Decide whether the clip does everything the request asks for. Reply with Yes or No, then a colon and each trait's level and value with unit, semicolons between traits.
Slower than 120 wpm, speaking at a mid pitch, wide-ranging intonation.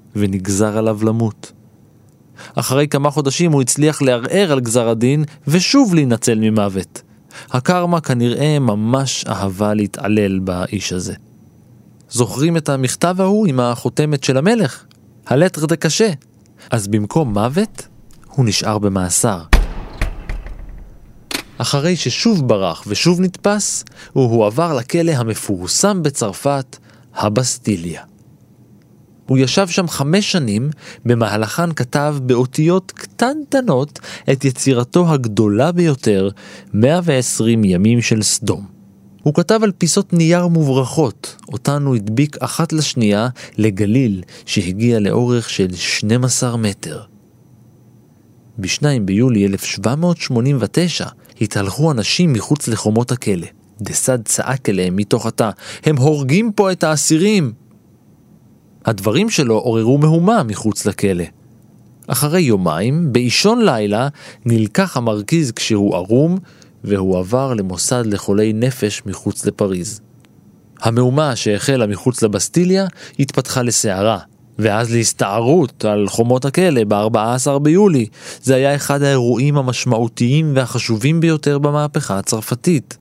No: average, 105 wpm; low, 125 Hz; wide, 5.9 semitones